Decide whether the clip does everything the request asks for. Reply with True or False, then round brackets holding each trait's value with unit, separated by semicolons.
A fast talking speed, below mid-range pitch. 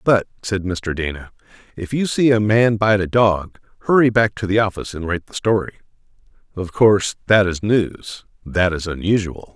False (180 wpm; 100 Hz)